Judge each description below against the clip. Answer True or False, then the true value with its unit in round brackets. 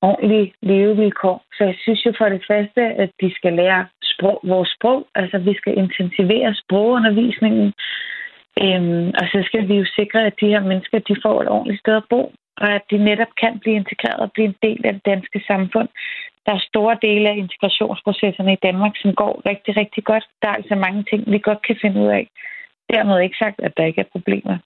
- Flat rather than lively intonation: True (2.1 semitones)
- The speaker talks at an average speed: True (210 wpm)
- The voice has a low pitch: False (205 Hz)